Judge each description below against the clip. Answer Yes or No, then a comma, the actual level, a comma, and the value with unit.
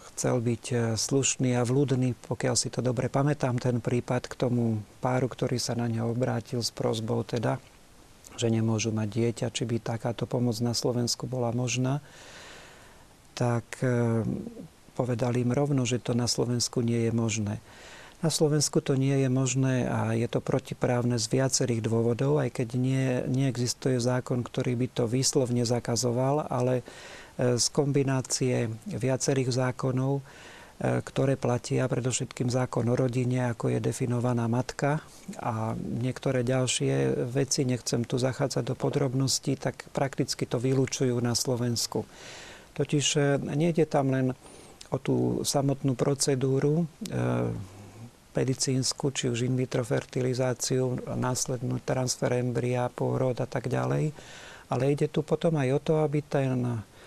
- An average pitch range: No, narrow, 2.1 semitones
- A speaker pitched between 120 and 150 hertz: Yes, low, 125 Hz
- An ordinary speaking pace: Yes, average, 135 wpm